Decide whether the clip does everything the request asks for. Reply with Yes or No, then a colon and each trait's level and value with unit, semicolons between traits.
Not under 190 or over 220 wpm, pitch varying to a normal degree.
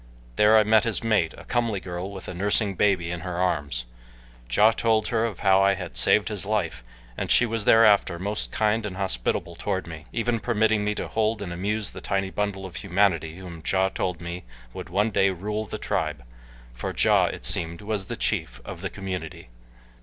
Yes: average, 200 wpm; average, 3.3 semitones